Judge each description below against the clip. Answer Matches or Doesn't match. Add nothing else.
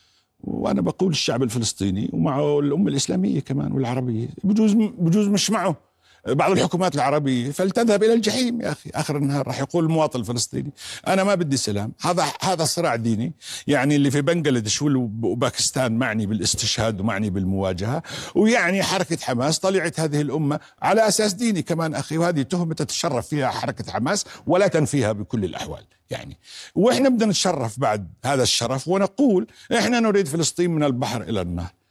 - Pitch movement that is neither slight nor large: Doesn't match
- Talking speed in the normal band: Doesn't match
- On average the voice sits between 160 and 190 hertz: Doesn't match